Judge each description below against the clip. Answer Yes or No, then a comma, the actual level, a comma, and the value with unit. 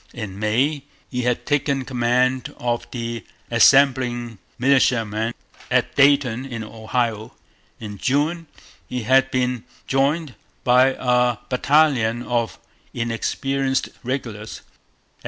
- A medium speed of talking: No, slow, 100 wpm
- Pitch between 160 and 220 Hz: No, low, 125 Hz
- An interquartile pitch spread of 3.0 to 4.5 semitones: No, narrow, 2.5 semitones